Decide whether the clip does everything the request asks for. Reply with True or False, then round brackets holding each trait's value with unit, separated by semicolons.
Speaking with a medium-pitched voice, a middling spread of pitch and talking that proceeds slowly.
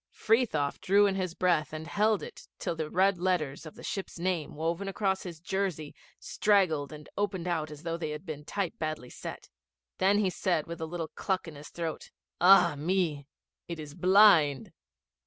False (170 Hz; 3.7 semitones; 185 wpm)